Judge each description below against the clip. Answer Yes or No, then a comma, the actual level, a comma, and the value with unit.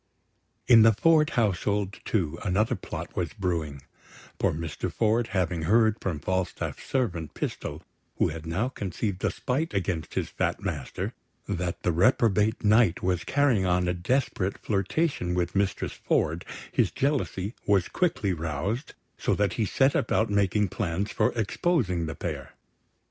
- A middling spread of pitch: Yes, average, 4.4 semitones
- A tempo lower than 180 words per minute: Yes, average, 150 wpm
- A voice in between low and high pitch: No, low, 100 Hz